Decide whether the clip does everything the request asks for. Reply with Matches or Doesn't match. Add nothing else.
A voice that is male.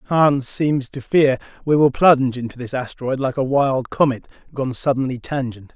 Matches